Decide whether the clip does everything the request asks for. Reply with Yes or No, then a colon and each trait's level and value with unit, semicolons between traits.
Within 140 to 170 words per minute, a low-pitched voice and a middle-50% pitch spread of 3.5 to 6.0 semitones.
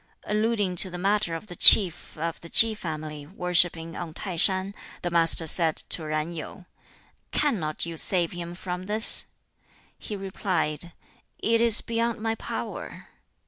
No: average, 150 wpm; medium, 180 Hz; average, 4.0 semitones